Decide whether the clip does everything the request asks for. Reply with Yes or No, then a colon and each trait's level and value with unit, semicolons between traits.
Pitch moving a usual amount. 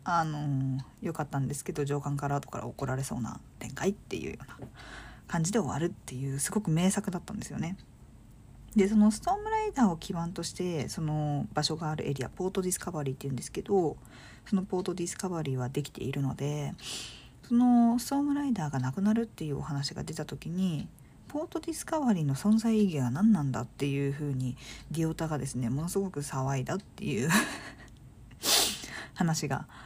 No: wide, 6.0 semitones